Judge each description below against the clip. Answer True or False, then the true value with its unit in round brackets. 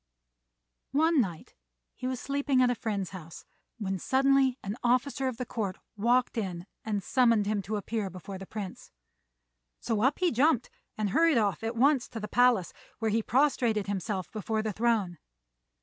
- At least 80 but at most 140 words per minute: False (170 wpm)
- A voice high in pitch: True (225 Hz)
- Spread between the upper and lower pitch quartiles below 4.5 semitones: True (4.1 semitones)